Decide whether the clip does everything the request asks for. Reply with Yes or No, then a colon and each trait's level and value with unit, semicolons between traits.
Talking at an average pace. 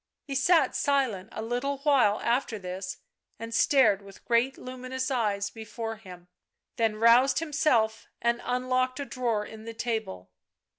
Yes: average, 145 wpm